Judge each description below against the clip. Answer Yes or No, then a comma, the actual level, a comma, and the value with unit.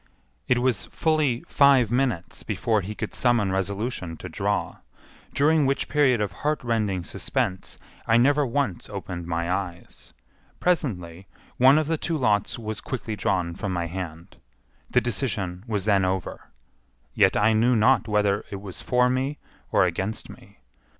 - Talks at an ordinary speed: Yes, average, 150 wpm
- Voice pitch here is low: Yes, low, 110 Hz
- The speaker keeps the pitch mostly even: No, average, 5.3 semitones